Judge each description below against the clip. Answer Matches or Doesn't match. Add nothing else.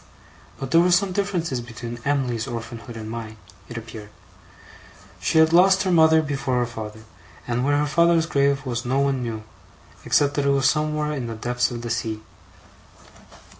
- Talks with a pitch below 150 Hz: Matches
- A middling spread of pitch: Matches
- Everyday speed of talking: Matches